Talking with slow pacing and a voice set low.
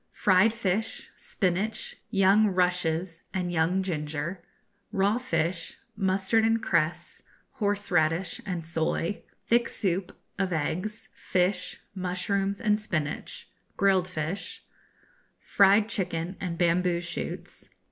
No: slow, 105 wpm; medium, 185 Hz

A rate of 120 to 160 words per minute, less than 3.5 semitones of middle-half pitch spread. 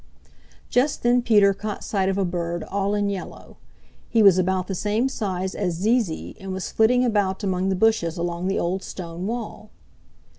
No: average, 185 wpm; average, 2.9 semitones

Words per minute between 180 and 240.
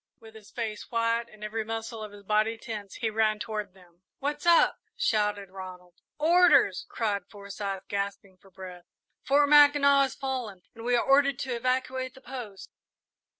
No: average, 165 wpm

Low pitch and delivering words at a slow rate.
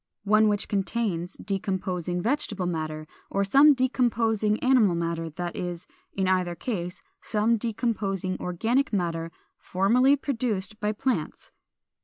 No: high, 200 Hz; slow, 120 wpm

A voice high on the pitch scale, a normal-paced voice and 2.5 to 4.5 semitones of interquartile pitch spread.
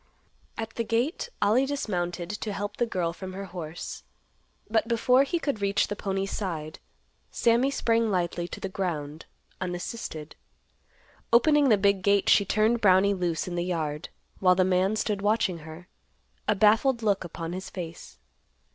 Yes: high, 195 Hz; average, 160 wpm; average, 4.1 semitones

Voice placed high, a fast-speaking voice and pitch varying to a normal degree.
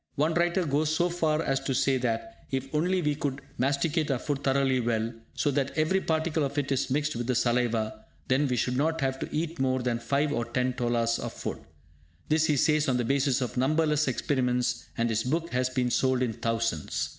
No: low, 135 Hz; fast, 215 wpm; average, 3.6 semitones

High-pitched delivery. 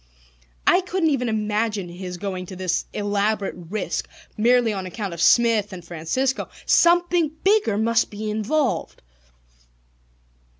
Yes: high, 215 Hz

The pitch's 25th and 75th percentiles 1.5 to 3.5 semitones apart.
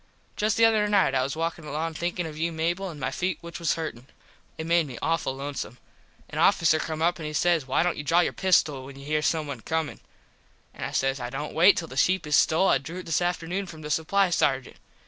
Yes: average, 3.2 semitones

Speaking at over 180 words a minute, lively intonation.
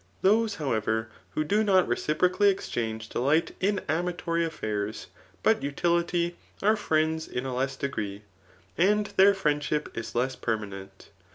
No: average, 140 wpm; wide, 8.0 semitones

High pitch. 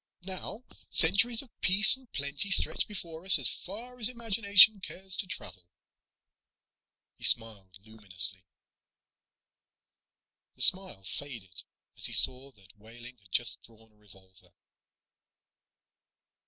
No: medium, 140 Hz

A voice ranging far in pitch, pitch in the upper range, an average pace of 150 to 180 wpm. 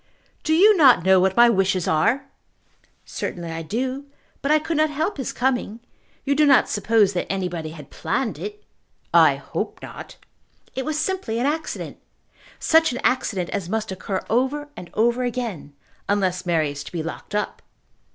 Yes: wide, 7.2 semitones; high, 230 Hz; average, 170 wpm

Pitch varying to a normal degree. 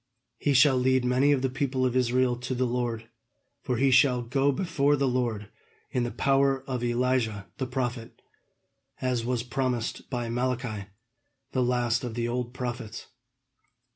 No: narrow, 1.6 semitones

